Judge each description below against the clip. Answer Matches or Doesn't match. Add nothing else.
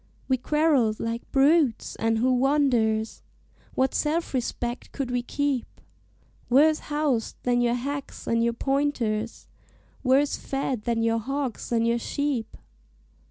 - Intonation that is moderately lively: Matches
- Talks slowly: Matches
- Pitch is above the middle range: Matches